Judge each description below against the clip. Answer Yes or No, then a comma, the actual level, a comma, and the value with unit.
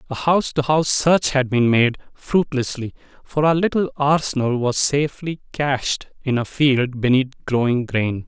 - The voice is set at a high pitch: No, low, 135 Hz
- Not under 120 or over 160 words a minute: Yes, average, 150 wpm